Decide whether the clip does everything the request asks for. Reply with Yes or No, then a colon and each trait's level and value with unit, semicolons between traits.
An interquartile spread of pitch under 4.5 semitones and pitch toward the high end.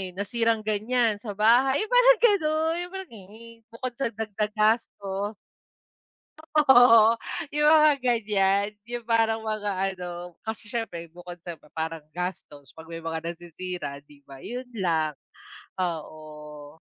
No: wide, 5.4 semitones; high, 210 Hz